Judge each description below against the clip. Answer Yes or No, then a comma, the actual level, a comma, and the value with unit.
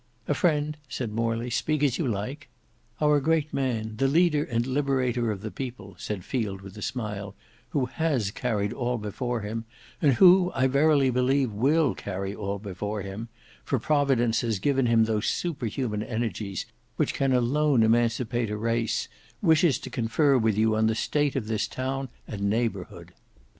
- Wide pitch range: No, average, 4.2 semitones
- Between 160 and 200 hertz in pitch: No, low, 120 Hz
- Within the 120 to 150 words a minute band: No, average, 170 wpm